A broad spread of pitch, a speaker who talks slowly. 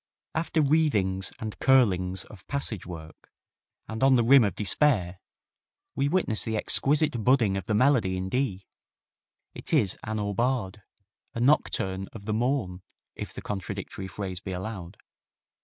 No: wide, 5.8 semitones; average, 145 wpm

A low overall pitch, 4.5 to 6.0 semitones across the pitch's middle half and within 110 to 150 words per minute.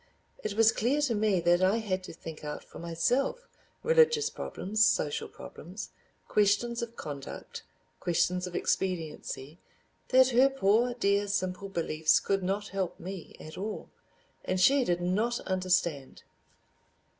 No: high, 195 Hz; average, 4.9 semitones; slow, 135 wpm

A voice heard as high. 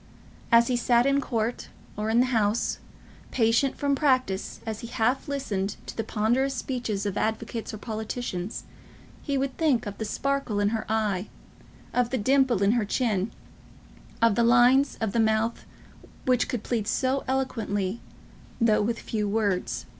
Yes: high, 230 Hz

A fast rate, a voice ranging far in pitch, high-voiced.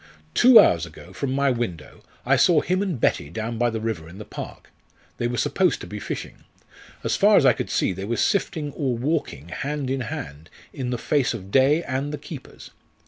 No: fast, 215 wpm; wide, 6.5 semitones; low, 125 Hz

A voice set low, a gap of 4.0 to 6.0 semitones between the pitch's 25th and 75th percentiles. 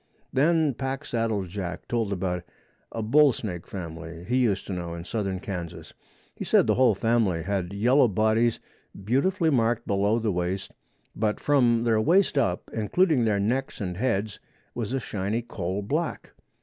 Yes: low, 110 Hz; average, 4.6 semitones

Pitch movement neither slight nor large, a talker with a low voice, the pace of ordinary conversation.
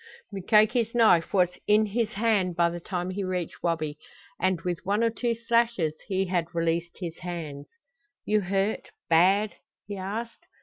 No: average, 3.9 semitones; high, 190 Hz; average, 160 wpm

